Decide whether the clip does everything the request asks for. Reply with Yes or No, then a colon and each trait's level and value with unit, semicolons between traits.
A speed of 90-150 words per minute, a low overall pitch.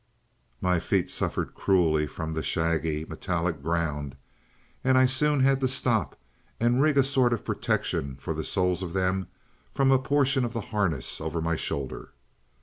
No: average, 165 wpm; very low, 90 Hz